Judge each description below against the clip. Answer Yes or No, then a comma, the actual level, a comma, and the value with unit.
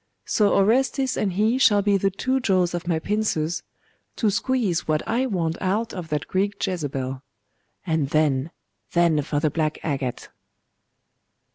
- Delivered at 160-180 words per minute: No, average, 150 wpm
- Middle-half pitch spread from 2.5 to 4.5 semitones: No, average, 5.3 semitones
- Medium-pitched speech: Yes, medium, 180 Hz